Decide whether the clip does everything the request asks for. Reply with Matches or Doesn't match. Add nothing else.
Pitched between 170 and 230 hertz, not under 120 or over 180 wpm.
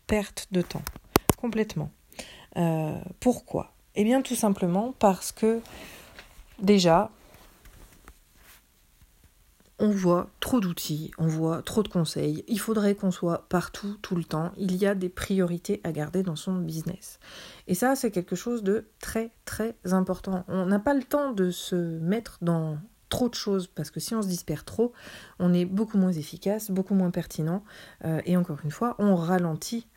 Matches